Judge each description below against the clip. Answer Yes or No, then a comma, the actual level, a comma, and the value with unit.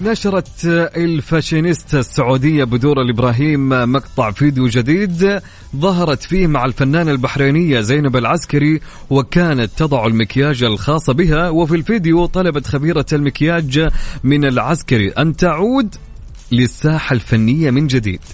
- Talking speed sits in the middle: Yes, average, 110 wpm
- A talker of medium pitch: Yes, medium, 145 Hz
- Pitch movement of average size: Yes, average, 4.3 semitones